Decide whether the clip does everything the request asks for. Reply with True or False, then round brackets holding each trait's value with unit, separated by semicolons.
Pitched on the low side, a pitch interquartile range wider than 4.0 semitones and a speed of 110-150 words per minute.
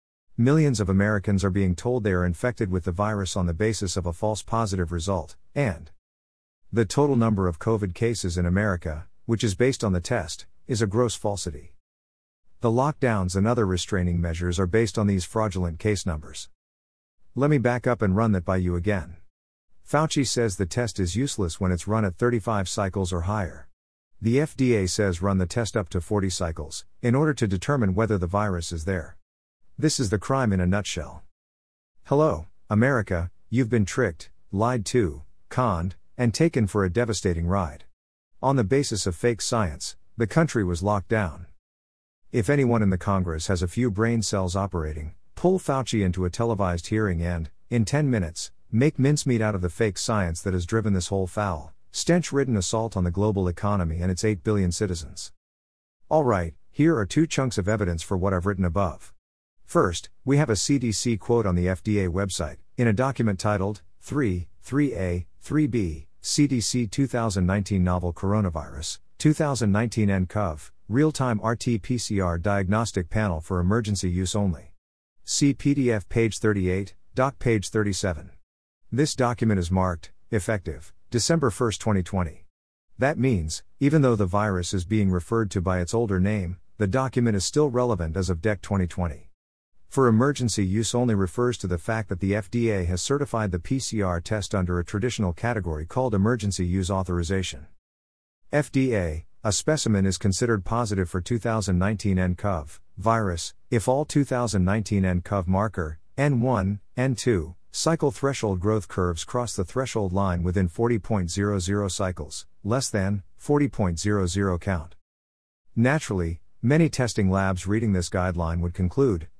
False (100 Hz; 4.6 semitones; 160 wpm)